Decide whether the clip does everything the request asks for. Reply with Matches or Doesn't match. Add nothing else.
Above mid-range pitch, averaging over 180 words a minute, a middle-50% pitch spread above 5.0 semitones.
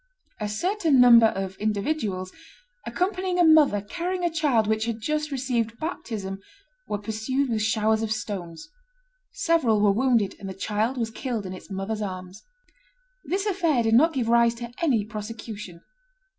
Doesn't match